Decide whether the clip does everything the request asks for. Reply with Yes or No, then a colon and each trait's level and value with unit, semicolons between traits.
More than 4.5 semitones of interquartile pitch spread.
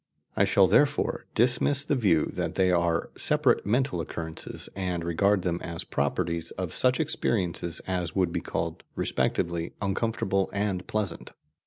No: average, 3.8 semitones